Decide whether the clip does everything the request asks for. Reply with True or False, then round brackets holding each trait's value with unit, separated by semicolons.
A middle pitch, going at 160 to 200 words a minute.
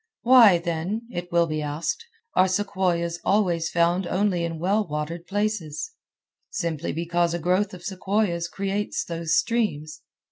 False (175 Hz; 140 wpm)